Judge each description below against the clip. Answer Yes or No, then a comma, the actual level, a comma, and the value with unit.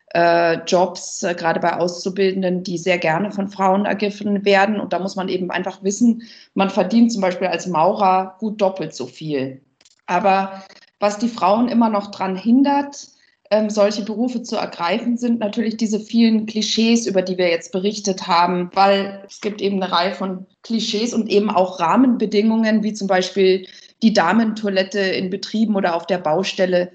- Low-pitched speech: No, high, 195 Hz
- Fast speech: No, average, 165 wpm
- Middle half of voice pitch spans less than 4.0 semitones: Yes, average, 2.7 semitones